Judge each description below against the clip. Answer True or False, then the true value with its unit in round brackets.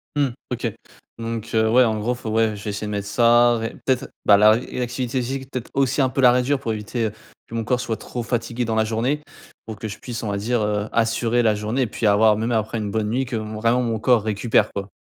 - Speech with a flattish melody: True (2.3 semitones)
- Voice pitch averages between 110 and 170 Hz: True (115 Hz)